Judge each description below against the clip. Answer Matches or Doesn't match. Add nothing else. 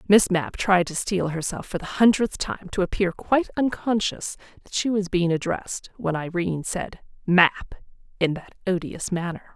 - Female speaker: Matches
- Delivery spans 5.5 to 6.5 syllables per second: Doesn't match